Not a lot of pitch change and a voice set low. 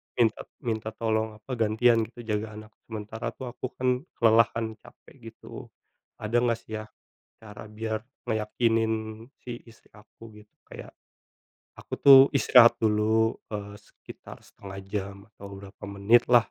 Yes: narrow, 1.6 semitones; low, 110 Hz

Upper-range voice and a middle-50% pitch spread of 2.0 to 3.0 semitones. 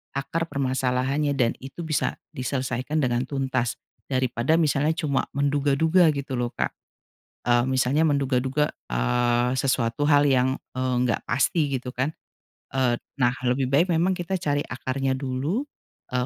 No: low, 135 Hz; narrow, 2.5 semitones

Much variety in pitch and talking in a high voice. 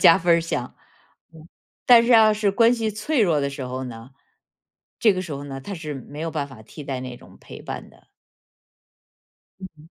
No: wide, 7.3 semitones; medium, 160 Hz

